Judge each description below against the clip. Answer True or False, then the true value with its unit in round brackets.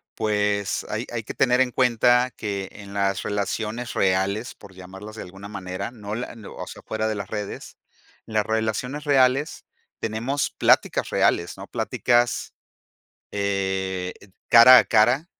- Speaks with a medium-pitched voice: False (110 Hz)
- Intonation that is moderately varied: True (3.5 semitones)